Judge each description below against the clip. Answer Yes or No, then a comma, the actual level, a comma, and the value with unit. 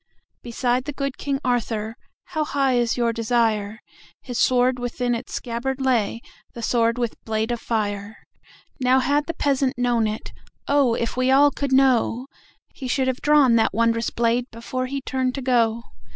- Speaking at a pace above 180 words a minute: No, average, 145 wpm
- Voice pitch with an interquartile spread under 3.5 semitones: Yes, narrow, 2.4 semitones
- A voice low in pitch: No, high, 245 Hz